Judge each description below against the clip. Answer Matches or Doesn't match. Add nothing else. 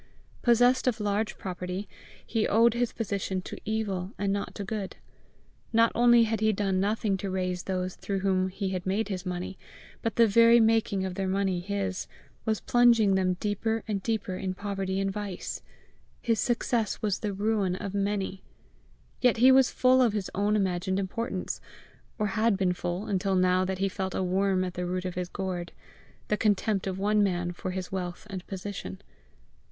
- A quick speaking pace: Doesn't match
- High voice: Matches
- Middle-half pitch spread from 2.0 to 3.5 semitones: Matches